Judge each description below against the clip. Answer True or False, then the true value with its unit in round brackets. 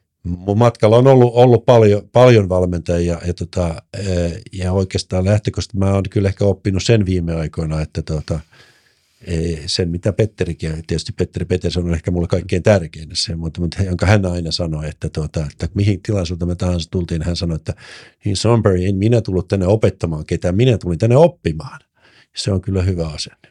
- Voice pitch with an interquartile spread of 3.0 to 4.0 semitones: True (3.3 semitones)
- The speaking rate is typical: False (180 wpm)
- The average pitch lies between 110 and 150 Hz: False (90 Hz)